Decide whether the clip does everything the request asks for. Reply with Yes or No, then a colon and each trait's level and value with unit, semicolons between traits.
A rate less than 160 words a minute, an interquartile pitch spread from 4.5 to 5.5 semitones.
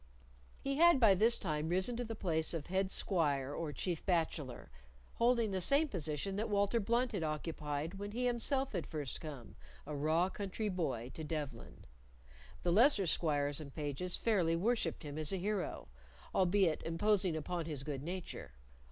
No: average, 170 wpm; average, 5.2 semitones